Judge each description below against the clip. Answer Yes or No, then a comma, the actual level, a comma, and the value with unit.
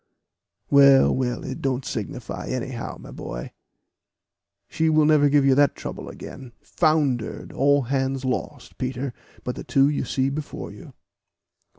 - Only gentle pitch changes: Yes, narrow, 1.9 semitones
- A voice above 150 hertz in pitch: No, low, 135 Hz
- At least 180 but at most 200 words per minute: No, average, 145 wpm